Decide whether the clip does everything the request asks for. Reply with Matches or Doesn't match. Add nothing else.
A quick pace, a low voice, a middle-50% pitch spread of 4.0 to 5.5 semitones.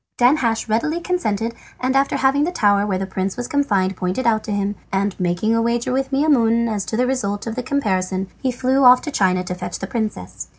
Doesn't match